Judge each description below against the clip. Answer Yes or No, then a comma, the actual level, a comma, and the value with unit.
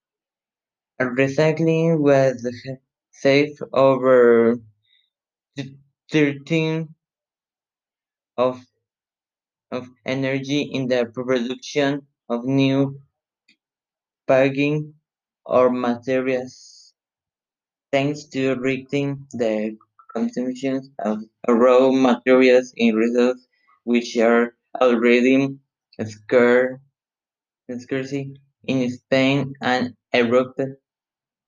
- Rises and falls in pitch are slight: Yes, narrow, 1.9 semitones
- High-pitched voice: No, low, 130 Hz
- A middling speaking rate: No, slow, 65 wpm